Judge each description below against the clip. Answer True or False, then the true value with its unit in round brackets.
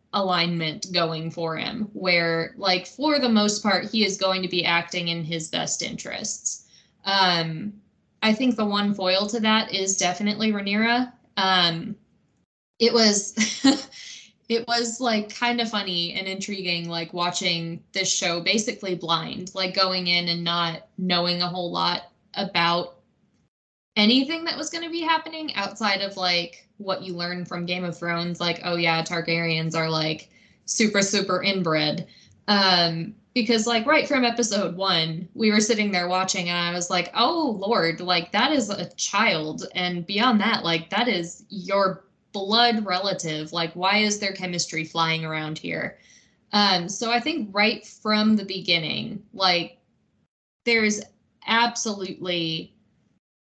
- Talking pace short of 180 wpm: True (150 wpm)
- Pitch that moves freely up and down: False (3.8 semitones)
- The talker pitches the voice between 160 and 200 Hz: True (190 Hz)